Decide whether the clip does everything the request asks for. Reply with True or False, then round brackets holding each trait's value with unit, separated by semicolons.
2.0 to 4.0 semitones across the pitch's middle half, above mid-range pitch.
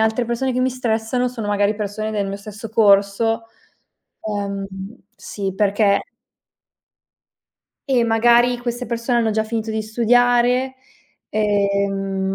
True (2.9 semitones; 220 Hz)